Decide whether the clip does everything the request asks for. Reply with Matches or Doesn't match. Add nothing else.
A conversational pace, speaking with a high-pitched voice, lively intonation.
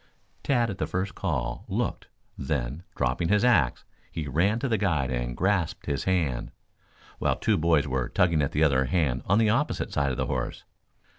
Doesn't match